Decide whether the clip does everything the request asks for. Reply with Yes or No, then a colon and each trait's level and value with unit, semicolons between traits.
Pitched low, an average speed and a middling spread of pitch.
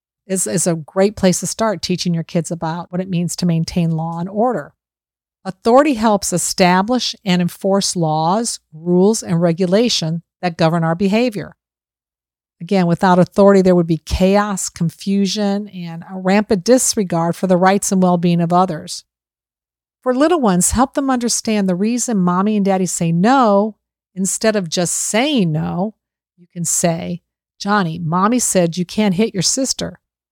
No: medium, 185 Hz; average, 160 wpm; average, 3.5 semitones